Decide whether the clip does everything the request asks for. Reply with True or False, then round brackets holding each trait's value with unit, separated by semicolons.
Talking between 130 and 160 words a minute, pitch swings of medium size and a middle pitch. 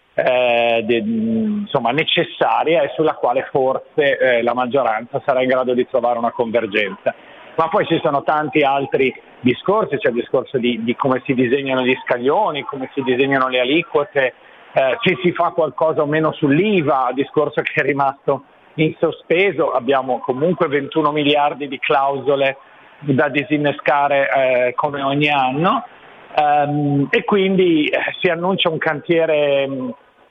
True (145 wpm; 3.6 semitones; 145 Hz)